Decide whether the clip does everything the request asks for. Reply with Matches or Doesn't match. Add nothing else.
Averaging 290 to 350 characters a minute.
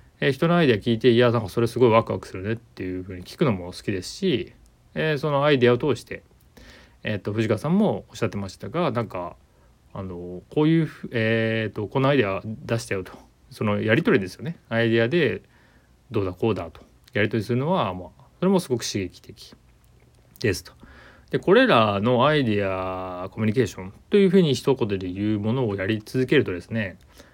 Doesn't match